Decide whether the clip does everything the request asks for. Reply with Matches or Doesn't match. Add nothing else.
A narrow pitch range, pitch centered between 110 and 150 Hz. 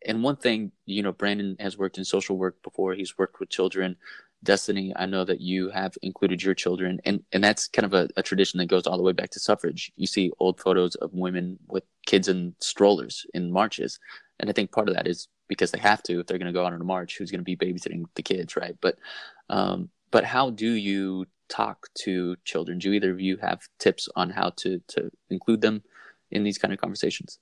Doesn't match